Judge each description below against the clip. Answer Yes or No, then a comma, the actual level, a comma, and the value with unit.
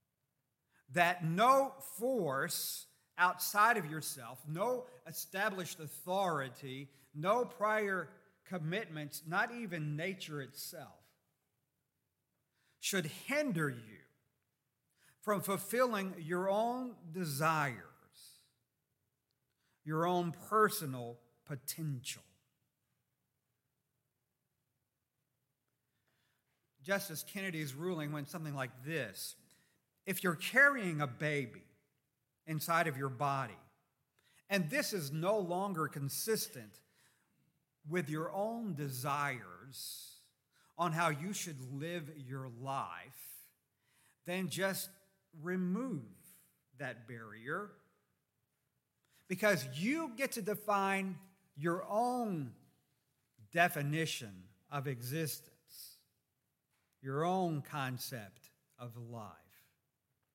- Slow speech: Yes, slow, 80 wpm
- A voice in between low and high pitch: Yes, medium, 155 Hz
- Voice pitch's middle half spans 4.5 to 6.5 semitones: Yes, wide, 5.6 semitones